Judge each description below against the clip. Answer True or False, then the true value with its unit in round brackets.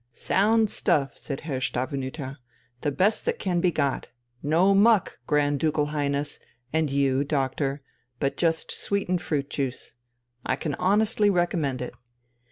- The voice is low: False (150 Hz)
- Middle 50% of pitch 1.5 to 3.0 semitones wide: False (4.8 semitones)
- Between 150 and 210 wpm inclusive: False (140 wpm)